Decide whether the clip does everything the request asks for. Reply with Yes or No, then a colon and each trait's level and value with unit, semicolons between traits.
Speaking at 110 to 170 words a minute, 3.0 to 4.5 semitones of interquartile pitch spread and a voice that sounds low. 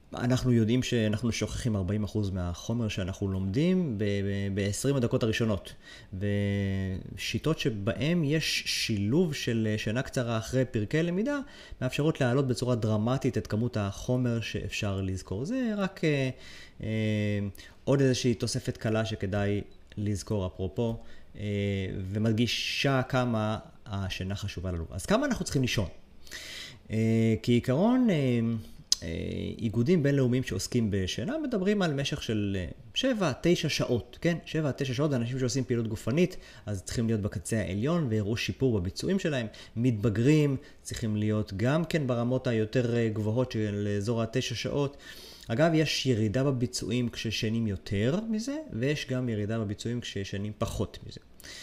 Yes: average, 125 wpm; average, 4.0 semitones; low, 115 Hz